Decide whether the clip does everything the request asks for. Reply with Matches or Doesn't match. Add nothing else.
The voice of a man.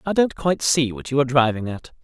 Matches